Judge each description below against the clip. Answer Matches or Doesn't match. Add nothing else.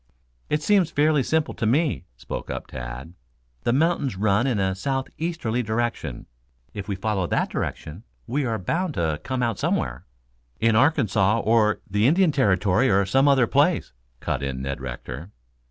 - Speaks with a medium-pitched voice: Doesn't match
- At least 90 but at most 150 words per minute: Doesn't match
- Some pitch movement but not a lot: Doesn't match